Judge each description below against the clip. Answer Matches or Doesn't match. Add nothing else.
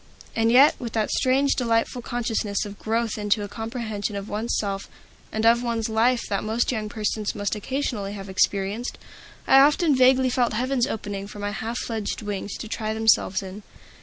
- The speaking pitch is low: Doesn't match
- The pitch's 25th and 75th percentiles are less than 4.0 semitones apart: Matches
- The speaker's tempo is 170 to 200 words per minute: Matches